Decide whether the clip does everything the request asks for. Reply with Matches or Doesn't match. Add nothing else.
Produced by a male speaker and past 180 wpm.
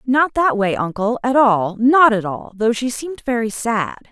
Doesn't match